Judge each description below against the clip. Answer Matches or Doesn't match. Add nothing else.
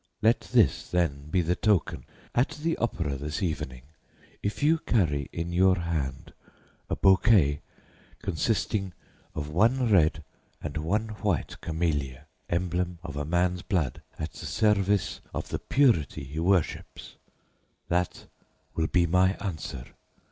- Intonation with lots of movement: Doesn't match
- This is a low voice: Matches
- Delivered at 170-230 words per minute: Doesn't match